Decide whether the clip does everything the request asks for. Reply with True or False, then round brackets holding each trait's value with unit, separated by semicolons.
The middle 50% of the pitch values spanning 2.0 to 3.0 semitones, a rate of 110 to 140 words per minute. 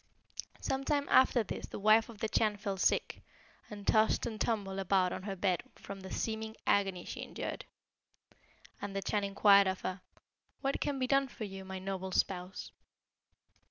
False (2.4 semitones; 175 wpm)